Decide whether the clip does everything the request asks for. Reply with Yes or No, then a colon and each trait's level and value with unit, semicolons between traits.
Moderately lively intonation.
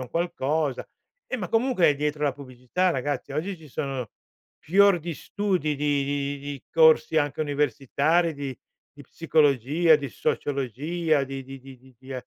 Yes: average, 3.2 semitones